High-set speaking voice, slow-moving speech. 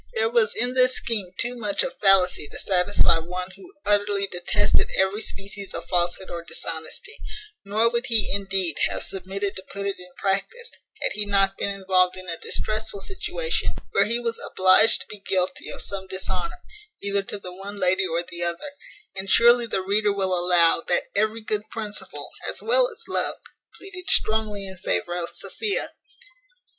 No: high, 200 Hz; average, 175 wpm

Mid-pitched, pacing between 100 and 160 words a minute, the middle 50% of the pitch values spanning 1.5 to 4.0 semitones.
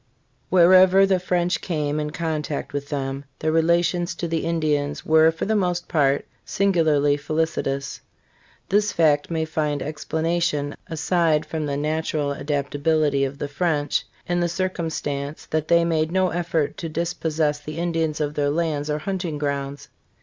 Yes: medium, 155 Hz; average, 155 wpm; average, 2.7 semitones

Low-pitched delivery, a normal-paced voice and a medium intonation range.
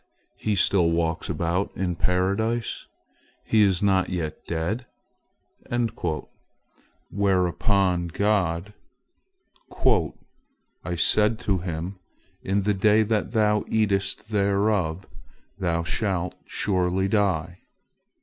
No: very low, 95 Hz; slow, 90 wpm; average, 3.2 semitones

